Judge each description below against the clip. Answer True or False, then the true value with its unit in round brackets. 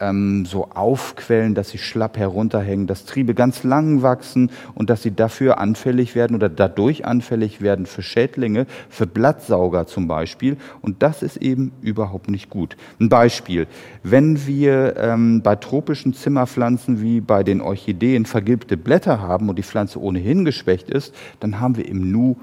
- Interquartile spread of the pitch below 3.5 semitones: False (4.2 semitones)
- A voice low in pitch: True (115 Hz)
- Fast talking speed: False (160 wpm)